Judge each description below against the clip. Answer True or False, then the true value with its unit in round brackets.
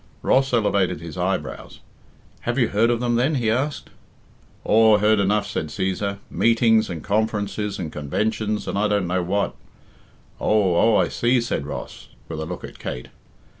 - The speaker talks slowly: False (170 wpm)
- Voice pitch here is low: True (105 Hz)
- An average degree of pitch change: True (3.6 semitones)